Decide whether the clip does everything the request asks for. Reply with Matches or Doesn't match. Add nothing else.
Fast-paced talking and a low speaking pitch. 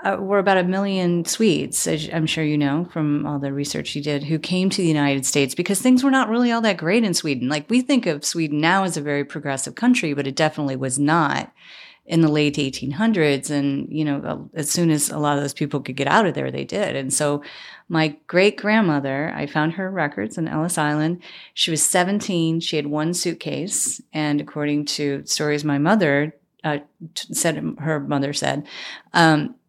Doesn't match